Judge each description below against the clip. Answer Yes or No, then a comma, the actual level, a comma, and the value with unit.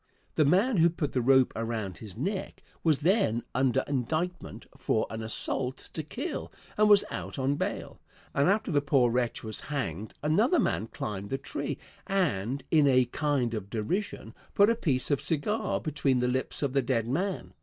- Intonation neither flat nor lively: No, wide, 6.1 semitones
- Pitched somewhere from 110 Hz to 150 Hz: Yes, medium, 140 Hz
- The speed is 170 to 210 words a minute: Yes, average, 180 wpm